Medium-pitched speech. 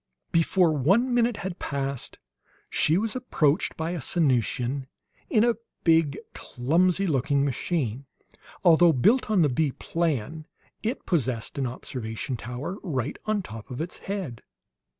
Yes: medium, 155 Hz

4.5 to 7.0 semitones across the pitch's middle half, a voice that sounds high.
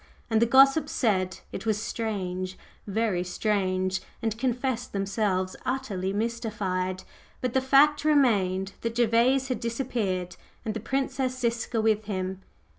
Yes: average, 4.8 semitones; high, 220 Hz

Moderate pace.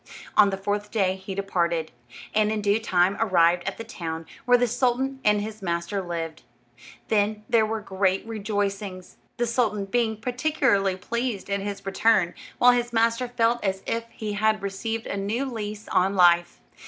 Yes: average, 170 wpm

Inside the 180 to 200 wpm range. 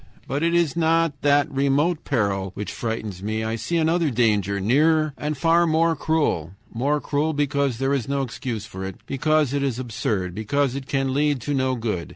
Yes: average, 195 wpm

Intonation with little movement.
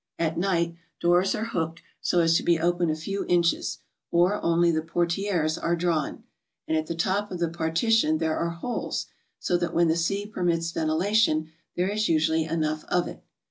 Yes: narrow, 1.8 semitones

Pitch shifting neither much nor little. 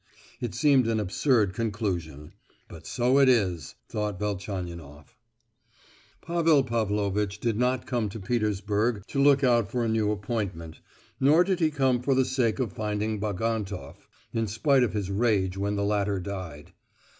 Yes: average, 4.0 semitones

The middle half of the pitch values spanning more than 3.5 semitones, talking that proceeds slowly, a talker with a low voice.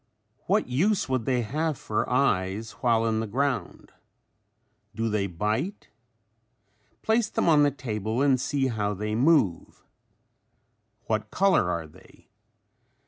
Yes: average, 5.2 semitones; slow, 130 wpm; low, 120 Hz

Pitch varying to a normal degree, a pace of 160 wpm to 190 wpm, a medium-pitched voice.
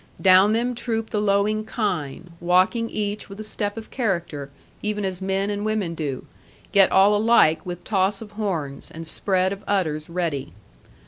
No: average, 3.4 semitones; average, 170 wpm; high, 195 Hz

